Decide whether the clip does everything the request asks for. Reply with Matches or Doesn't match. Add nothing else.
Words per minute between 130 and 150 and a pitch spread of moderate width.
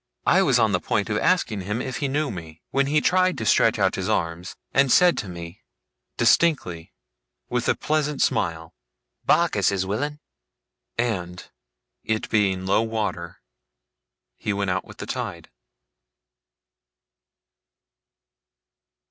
Doesn't match